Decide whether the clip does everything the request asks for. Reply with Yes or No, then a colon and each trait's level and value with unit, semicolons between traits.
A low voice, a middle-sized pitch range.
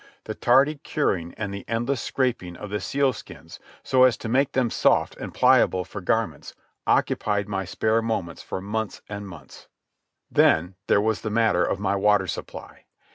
Yes: low, 105 Hz; average, 3.8 semitones